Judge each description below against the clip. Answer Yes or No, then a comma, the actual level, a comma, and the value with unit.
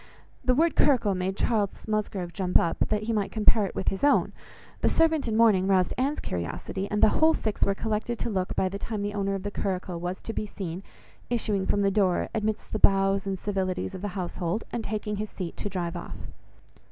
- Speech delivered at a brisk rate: Yes, fast, 220 wpm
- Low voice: No, high, 200 Hz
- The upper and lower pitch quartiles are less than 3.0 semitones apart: Yes, narrow, 2.5 semitones